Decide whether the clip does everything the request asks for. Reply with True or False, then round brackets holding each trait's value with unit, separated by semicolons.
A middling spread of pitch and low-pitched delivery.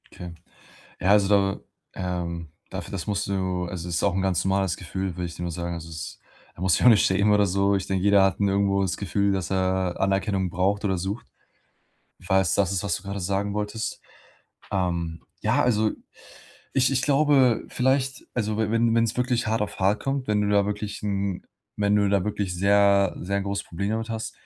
False (2.1 semitones; 100 Hz)